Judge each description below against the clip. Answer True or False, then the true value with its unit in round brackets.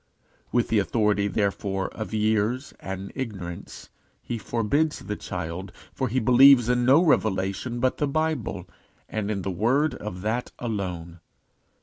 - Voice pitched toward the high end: False (110 Hz)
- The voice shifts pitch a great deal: False (4.3 semitones)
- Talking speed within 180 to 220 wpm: False (140 wpm)